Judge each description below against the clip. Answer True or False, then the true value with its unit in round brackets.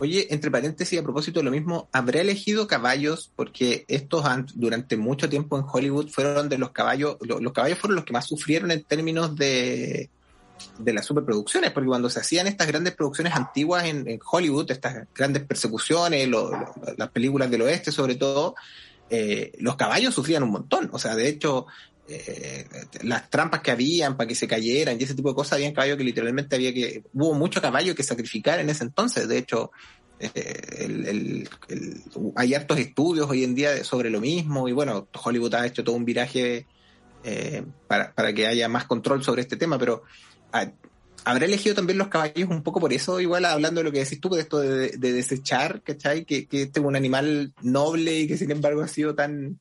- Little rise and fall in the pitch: False (4.1 semitones)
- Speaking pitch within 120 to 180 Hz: True (140 Hz)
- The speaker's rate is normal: False (205 wpm)